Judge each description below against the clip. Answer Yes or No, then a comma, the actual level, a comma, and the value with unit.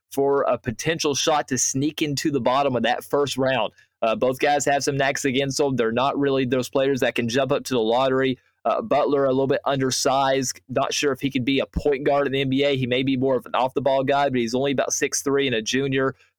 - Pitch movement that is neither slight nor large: No, narrow, 1.3 semitones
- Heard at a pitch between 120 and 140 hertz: Yes, low, 135 Hz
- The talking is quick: Yes, fast, 255 wpm